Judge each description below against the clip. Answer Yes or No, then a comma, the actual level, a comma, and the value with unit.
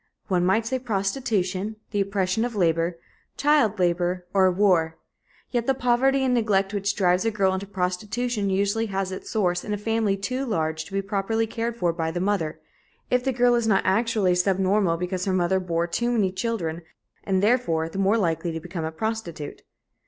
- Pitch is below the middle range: No, high, 195 Hz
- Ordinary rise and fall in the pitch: Yes, average, 3.9 semitones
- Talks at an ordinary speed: Yes, average, 190 wpm